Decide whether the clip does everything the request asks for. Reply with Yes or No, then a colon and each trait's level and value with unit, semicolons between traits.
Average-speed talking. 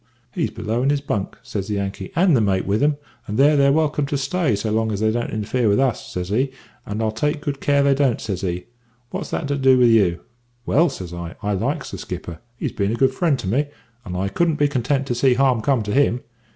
No: fast, 255 wpm